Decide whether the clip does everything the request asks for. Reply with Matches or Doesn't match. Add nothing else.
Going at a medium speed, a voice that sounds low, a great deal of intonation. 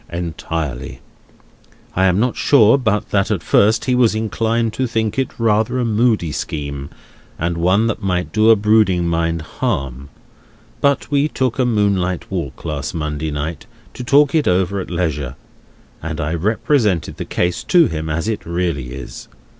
Matches